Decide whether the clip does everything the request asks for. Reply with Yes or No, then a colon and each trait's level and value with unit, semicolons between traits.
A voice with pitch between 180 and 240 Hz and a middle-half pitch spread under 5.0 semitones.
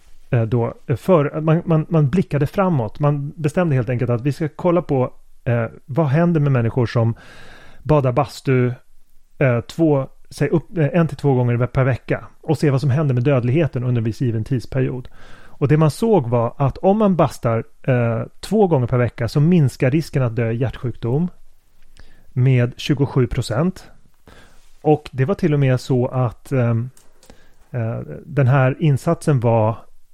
No: low, 135 Hz; average, 4.0 semitones